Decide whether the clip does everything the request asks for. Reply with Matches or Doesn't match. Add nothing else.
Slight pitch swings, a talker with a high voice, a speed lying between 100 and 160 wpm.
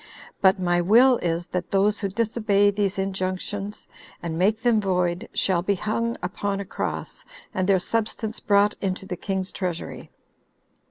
Matches